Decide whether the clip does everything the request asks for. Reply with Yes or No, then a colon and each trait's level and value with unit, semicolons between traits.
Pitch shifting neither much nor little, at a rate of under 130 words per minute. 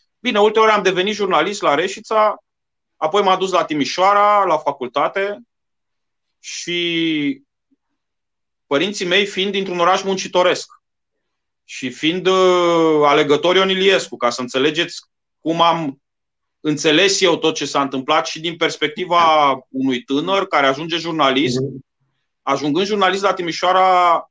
Yes: average, 4.5 semitones; average, 120 wpm